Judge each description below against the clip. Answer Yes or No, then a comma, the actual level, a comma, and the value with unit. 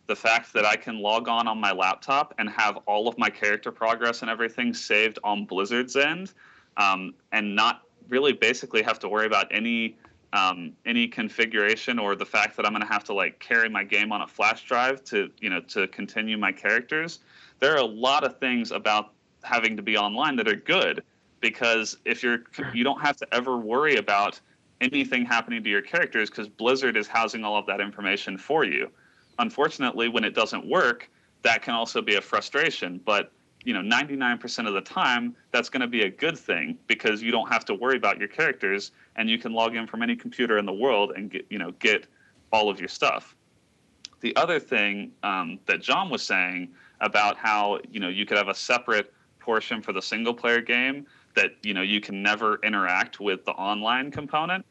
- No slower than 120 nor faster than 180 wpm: No, fast, 205 wpm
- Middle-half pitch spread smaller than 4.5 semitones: Yes, average, 2.9 semitones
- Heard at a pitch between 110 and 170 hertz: Yes, low, 115 Hz